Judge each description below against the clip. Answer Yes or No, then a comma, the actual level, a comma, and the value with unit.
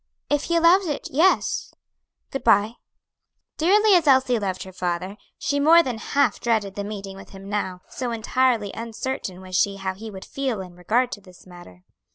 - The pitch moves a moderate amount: No, wide, 6.0 semitones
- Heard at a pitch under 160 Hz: No, high, 220 Hz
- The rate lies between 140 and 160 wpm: No, average, 185 wpm